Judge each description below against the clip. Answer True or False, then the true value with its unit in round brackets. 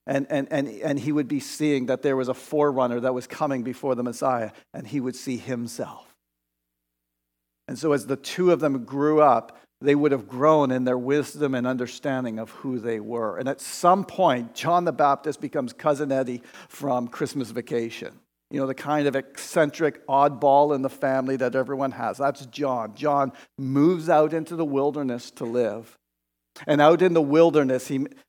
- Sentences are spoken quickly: False (185 wpm)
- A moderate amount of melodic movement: True (3.0 semitones)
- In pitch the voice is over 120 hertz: True (135 Hz)